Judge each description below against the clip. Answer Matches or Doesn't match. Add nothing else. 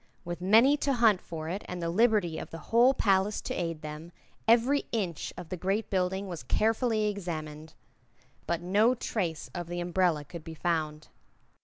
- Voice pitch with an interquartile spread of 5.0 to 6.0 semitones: Doesn't match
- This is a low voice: Doesn't match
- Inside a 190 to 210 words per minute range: Doesn't match